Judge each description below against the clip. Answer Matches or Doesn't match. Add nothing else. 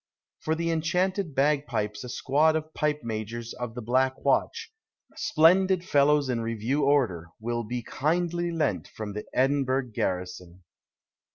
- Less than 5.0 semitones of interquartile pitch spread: Doesn't match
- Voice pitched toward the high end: Doesn't match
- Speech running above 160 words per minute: Doesn't match